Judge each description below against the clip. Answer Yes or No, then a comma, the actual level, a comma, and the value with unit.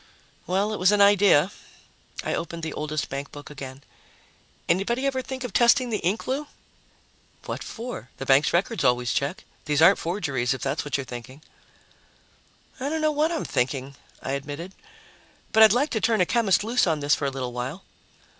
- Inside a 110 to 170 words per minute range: No, average, 185 wpm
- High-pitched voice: No, medium, 170 Hz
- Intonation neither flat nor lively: No, wide, 8.2 semitones